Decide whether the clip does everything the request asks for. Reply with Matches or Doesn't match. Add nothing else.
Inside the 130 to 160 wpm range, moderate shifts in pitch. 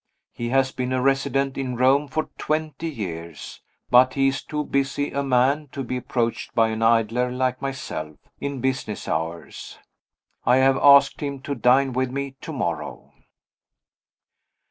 Doesn't match